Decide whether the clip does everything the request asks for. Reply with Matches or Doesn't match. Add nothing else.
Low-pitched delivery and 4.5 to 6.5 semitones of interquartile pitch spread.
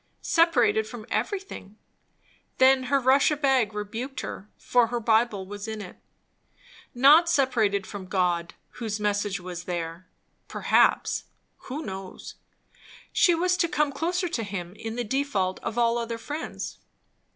Doesn't match